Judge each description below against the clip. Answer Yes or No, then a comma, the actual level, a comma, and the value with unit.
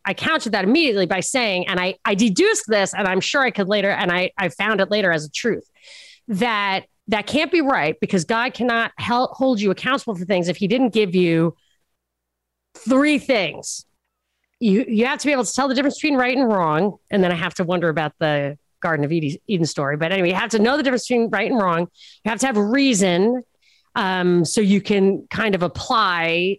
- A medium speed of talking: No, fast, 220 wpm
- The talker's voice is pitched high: Yes, high, 200 Hz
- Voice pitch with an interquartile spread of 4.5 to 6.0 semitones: Yes, average, 5.2 semitones